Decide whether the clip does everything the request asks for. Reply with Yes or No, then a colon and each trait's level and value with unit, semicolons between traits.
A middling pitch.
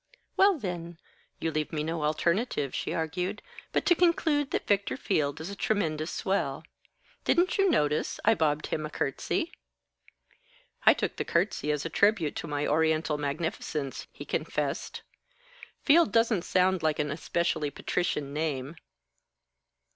Yes: medium, 165 Hz